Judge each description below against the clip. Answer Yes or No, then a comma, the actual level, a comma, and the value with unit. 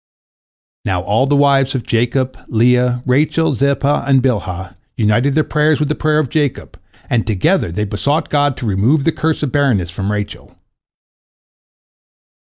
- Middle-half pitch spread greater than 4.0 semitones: Yes, average, 5.3 semitones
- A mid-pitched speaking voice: No, low, 130 Hz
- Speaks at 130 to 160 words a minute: Yes, average, 155 wpm